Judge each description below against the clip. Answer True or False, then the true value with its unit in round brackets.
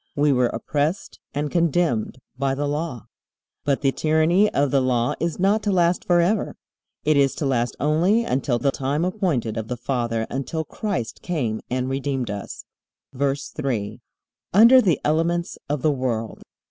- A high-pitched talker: False (145 Hz)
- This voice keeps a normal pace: True (160 wpm)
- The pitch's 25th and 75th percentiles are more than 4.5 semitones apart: True (5.0 semitones)